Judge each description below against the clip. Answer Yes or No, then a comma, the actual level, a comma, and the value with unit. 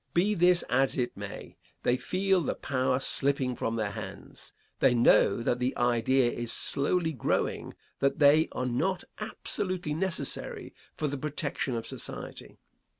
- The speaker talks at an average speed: Yes, average, 150 wpm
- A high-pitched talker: No, low, 135 Hz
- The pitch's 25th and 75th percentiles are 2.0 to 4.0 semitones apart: No, average, 5.3 semitones